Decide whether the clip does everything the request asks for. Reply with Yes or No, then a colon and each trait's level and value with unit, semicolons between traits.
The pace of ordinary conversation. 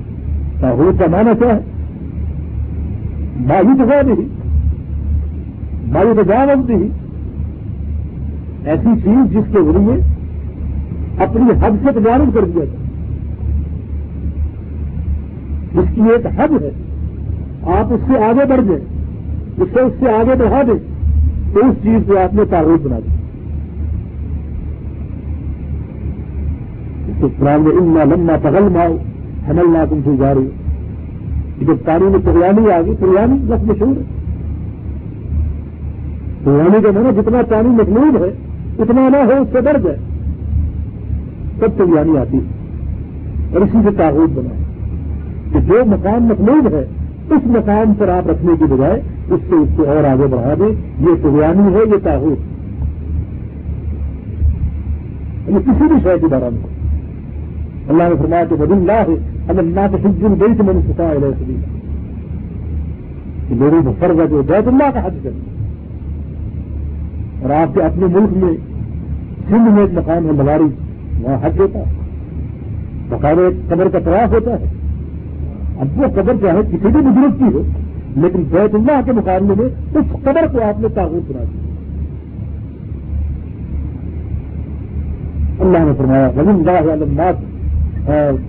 Yes: average, 130 wpm